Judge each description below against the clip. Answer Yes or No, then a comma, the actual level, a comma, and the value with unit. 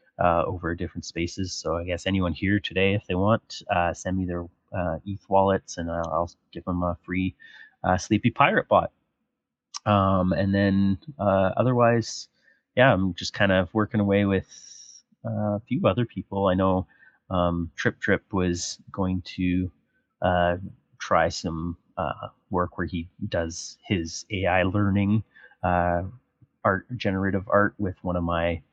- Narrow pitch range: Yes, narrow, 2.3 semitones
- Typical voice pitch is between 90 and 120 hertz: Yes, very low, 95 Hz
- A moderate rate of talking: Yes, average, 160 wpm